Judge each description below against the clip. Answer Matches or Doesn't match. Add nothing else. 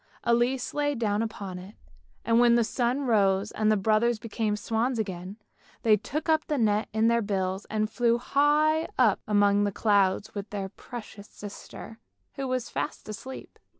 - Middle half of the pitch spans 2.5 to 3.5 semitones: Matches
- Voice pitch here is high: Matches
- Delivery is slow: Doesn't match